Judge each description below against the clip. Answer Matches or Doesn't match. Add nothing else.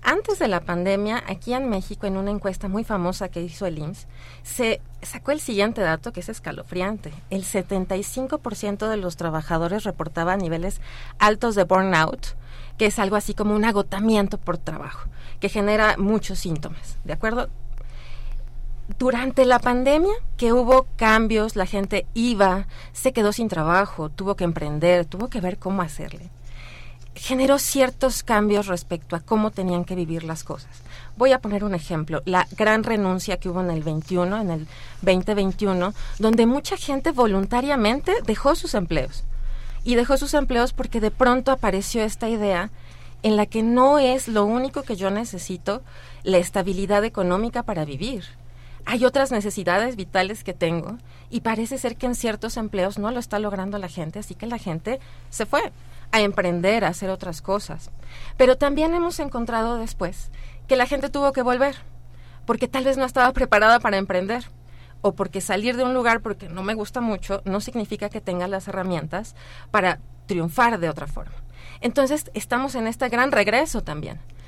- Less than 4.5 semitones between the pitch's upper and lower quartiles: Doesn't match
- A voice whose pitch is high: Matches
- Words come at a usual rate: Matches